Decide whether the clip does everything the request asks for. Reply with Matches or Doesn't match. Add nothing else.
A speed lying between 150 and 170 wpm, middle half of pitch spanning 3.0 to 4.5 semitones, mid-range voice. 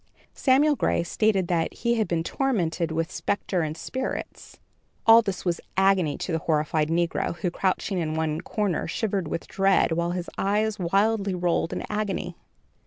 Matches